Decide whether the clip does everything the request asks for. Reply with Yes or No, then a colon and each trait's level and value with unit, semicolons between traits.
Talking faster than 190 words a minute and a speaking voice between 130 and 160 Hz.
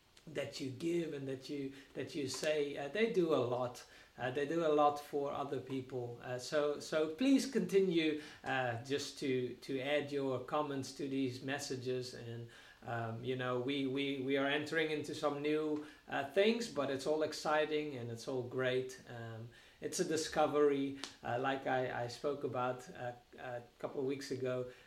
No: average, 180 wpm; medium, 140 Hz